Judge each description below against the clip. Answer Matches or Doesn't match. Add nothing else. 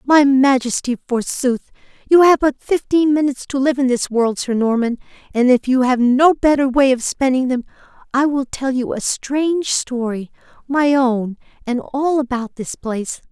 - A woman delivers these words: Matches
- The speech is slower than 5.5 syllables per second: Matches